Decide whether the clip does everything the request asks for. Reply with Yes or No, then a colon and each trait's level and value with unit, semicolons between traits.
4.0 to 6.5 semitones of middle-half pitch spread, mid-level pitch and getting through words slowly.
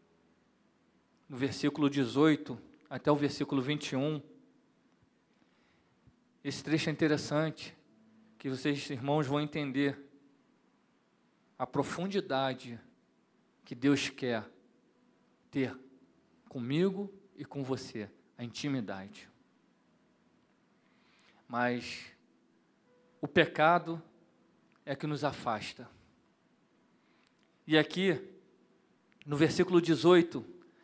No: average, 3.1 semitones; medium, 145 Hz; slow, 80 wpm